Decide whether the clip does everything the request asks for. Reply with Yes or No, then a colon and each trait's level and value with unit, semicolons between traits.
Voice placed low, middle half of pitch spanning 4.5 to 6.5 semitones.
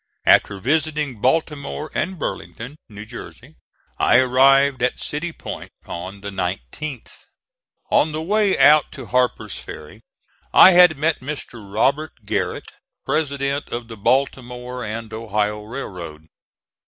Yes: low, 130 Hz; wide, 5.6 semitones